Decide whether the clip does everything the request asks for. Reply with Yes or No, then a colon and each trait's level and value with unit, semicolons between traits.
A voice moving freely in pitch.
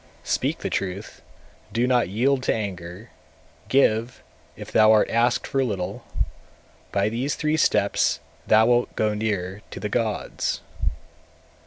No: average, 3.3 semitones